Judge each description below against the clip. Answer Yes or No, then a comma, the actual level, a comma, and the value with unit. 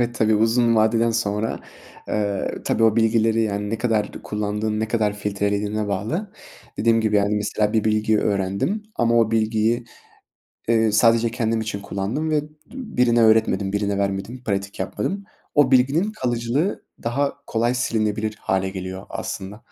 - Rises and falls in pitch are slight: Yes, narrow, 2.3 semitones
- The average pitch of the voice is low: Yes, low, 110 Hz